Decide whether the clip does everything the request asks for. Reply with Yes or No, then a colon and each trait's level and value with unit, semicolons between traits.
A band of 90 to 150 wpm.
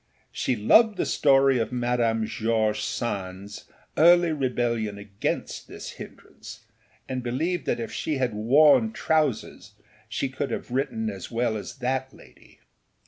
Yes: average, 140 wpm